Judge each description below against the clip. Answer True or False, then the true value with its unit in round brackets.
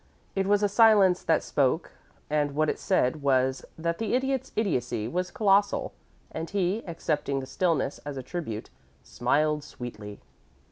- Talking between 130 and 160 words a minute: True (150 wpm)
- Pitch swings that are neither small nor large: False (6.2 semitones)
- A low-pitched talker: False (160 Hz)